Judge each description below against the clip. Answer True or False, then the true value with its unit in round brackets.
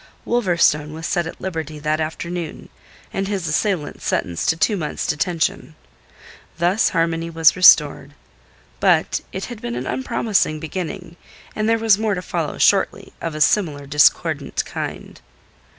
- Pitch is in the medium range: True (165 Hz)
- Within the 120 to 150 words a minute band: True (145 wpm)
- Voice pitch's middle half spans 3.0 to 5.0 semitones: True (4.0 semitones)